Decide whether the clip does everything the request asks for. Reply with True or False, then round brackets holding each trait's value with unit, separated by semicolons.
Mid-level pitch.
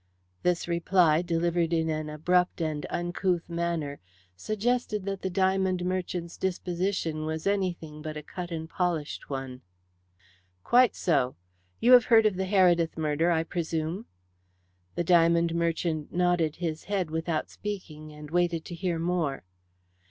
True (170 Hz)